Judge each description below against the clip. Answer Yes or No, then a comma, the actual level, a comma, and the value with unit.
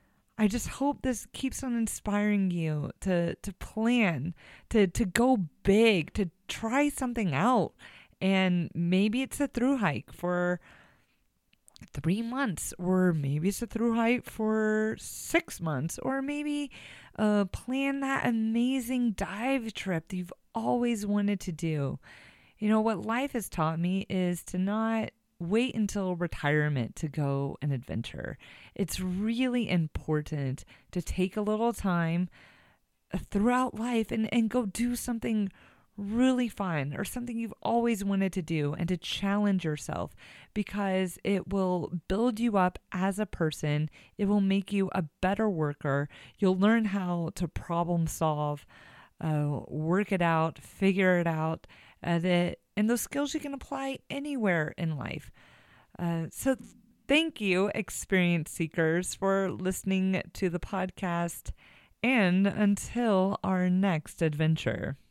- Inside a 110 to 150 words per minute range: Yes, average, 140 wpm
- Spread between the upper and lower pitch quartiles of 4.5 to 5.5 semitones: Yes, average, 4.9 semitones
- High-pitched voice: Yes, high, 195 Hz